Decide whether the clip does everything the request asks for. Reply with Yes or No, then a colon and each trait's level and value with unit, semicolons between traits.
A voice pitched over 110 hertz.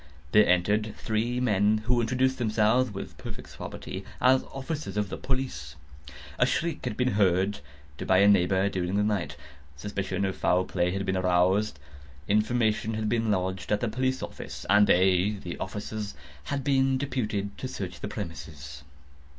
No: low, 105 Hz